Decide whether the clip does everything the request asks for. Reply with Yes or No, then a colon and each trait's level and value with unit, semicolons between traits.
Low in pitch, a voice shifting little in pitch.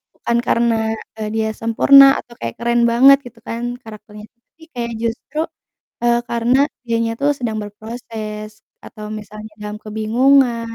No: high, 230 Hz; narrow, 1.8 semitones